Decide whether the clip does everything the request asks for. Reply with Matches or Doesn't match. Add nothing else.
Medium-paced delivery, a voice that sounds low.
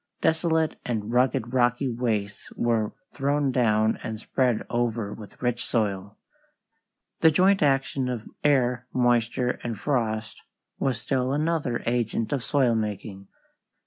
Doesn't match